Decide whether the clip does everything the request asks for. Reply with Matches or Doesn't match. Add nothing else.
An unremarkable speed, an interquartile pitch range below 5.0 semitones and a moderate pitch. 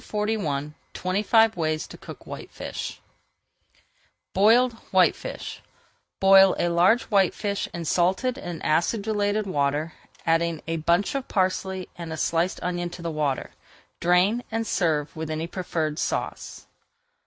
Doesn't match